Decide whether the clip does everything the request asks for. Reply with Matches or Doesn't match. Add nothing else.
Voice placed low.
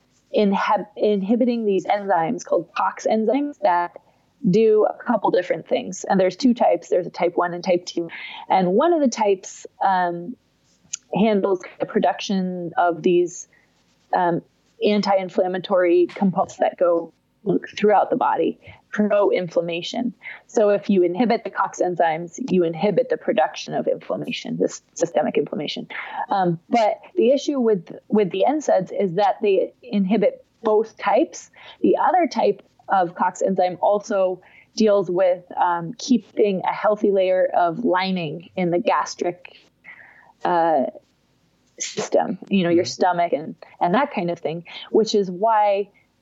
Doesn't match